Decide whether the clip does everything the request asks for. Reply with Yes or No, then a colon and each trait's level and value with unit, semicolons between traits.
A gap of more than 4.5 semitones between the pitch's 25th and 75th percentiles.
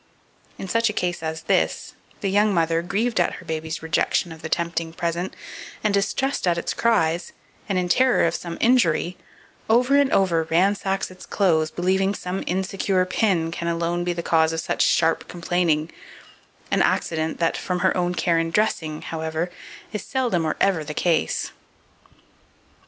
No: average, 3.0 semitones